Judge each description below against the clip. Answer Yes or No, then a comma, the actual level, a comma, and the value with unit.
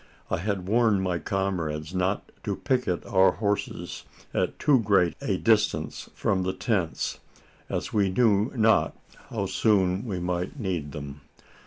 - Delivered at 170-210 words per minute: No, average, 145 wpm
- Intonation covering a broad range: No, average, 3.0 semitones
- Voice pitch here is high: No, very low, 95 Hz